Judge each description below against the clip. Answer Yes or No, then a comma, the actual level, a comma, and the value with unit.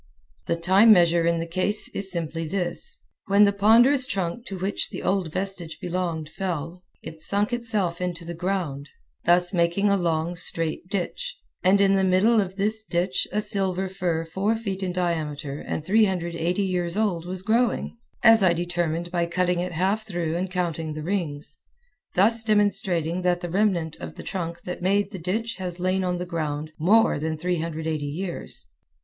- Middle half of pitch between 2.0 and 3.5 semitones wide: Yes, average, 2.8 semitones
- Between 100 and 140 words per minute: No, average, 175 wpm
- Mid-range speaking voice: Yes, medium, 180 Hz